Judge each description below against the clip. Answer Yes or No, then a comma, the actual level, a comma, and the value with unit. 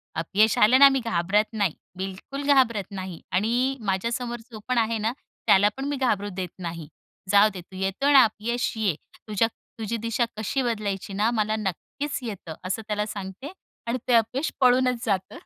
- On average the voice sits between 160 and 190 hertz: No, high, 215 Hz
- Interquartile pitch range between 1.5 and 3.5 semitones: No, average, 4.2 semitones